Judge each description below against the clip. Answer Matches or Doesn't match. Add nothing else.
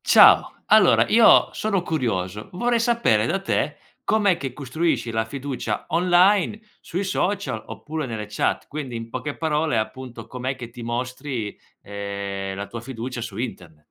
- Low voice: Matches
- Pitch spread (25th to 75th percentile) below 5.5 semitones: Doesn't match